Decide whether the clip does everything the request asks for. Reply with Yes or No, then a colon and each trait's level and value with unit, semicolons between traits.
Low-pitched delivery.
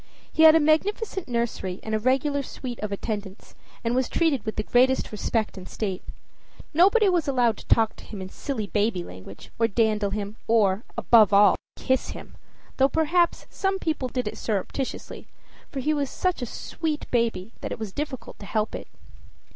No: high, 235 Hz